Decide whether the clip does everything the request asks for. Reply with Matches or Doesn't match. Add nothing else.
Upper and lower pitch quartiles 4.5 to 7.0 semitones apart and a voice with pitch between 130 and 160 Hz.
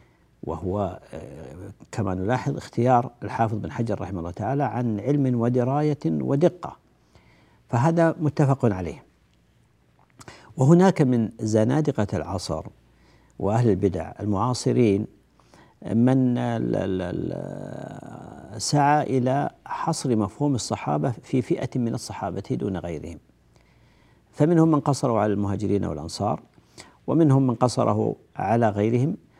Doesn't match